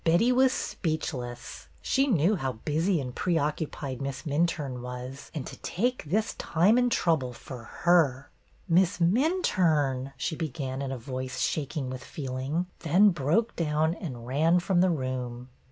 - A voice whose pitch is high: No, medium, 150 Hz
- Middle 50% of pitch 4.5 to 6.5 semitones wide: Yes, average, 5.2 semitones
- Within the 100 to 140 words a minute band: No, average, 160 wpm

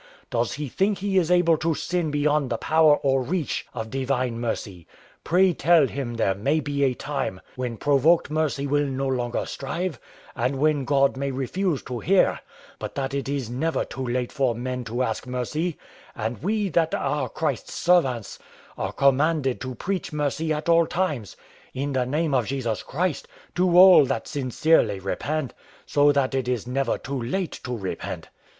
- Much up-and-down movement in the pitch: No, average, 4.0 semitones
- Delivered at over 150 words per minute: Yes, average, 180 wpm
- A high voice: No, medium, 140 Hz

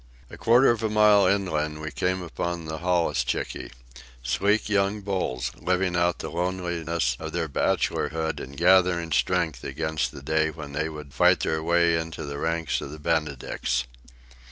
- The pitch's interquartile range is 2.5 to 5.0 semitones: Yes, average, 3.5 semitones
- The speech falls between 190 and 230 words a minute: No, average, 155 wpm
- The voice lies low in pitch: Yes, very low, 80 Hz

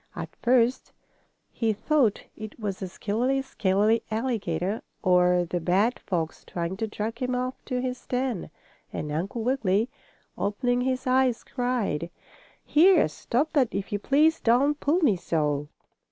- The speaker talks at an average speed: Yes, average, 145 wpm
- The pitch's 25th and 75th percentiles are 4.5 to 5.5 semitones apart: Yes, average, 5.2 semitones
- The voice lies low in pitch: No, high, 230 Hz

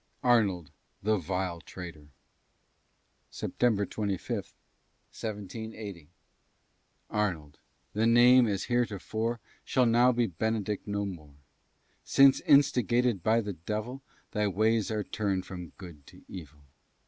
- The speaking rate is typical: No, slow, 110 wpm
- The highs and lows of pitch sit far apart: No, average, 4.1 semitones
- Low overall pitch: Yes, low, 105 Hz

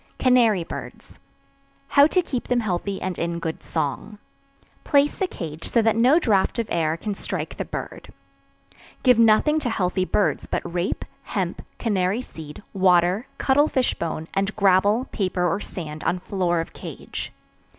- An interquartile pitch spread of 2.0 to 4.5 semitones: No, wide, 5.5 semitones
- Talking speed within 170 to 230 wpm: No, average, 160 wpm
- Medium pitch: No, high, 195 Hz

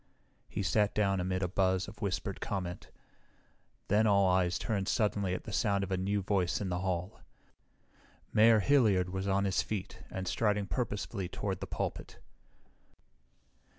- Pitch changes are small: Yes, narrow, 2.0 semitones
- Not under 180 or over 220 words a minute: No, average, 155 wpm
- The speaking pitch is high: No, low, 100 Hz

